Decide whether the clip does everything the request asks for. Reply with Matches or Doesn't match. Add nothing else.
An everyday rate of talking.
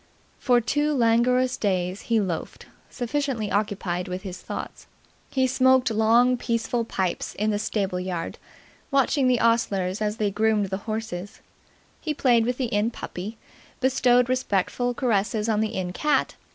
Matches